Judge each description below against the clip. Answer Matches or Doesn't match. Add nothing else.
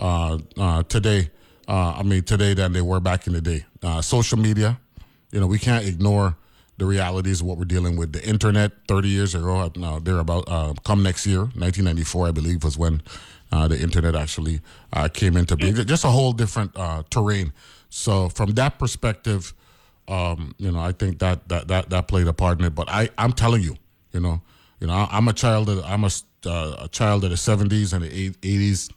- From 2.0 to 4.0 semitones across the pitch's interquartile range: Matches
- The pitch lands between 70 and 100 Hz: Matches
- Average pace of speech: Doesn't match